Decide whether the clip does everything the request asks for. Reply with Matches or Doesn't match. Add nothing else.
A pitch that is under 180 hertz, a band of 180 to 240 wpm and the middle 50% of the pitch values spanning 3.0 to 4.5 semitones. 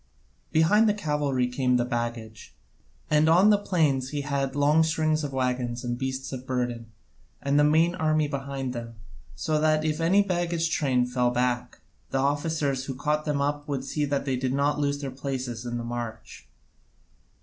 Matches